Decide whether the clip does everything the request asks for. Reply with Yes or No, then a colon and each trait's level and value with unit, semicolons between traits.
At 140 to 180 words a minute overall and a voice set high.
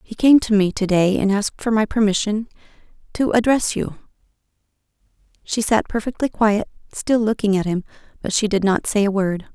Yes: average, 175 wpm; high, 210 Hz